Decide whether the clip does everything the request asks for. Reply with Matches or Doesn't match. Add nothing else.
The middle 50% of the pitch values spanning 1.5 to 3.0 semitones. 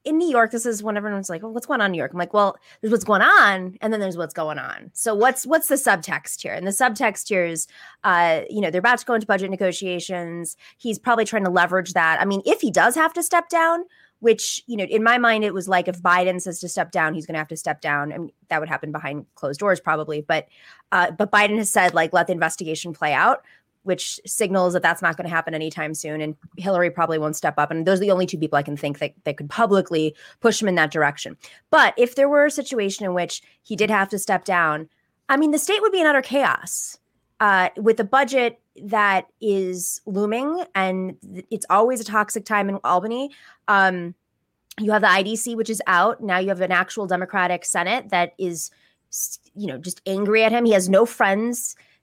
Doesn't match